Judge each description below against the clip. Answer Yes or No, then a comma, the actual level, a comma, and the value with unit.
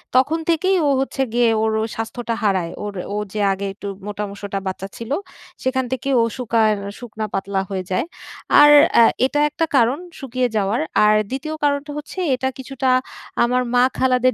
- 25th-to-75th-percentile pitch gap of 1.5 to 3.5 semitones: No, average, 4.2 semitones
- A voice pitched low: No, high, 245 Hz